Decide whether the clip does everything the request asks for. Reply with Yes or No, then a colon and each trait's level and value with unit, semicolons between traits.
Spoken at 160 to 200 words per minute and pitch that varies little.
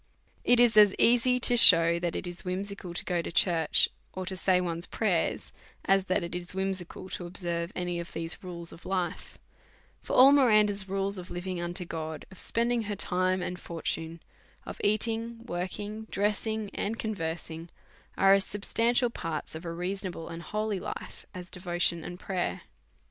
No: average, 175 wpm; average, 3.3 semitones